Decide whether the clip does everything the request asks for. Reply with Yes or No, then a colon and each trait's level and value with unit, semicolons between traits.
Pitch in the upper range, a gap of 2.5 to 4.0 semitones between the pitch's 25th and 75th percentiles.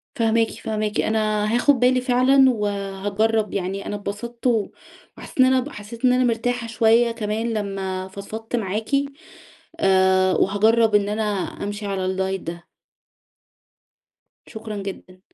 Yes: high, 215 Hz; average, 2.8 semitones